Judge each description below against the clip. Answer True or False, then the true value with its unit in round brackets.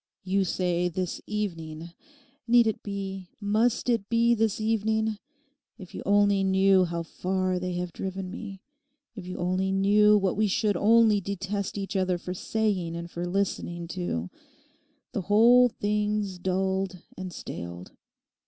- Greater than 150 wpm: False (145 wpm)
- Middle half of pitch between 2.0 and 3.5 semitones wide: True (2.6 semitones)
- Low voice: False (195 Hz)